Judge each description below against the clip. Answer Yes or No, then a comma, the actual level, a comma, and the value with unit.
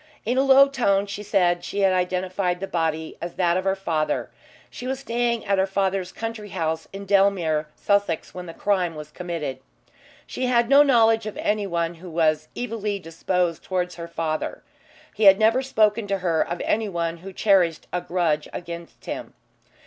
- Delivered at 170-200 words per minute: Yes, average, 180 wpm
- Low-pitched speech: No, high, 190 Hz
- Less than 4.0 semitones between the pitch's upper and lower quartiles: Yes, average, 3.6 semitones